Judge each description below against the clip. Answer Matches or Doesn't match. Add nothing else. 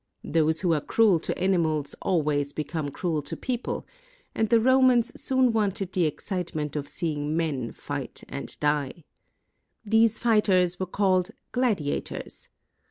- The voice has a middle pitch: Matches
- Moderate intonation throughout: Doesn't match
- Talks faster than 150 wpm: Doesn't match